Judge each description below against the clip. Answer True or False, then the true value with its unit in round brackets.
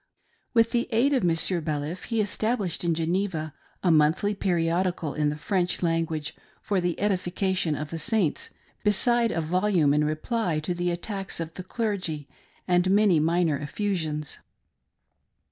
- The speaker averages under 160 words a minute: True (150 wpm)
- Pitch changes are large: False (4.3 semitones)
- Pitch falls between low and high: True (175 Hz)